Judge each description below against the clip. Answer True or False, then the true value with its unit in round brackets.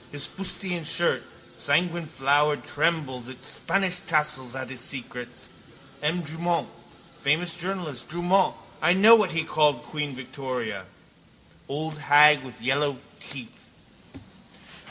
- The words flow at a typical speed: False (115 wpm)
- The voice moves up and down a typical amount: True (4.5 semitones)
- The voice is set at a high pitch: False (150 Hz)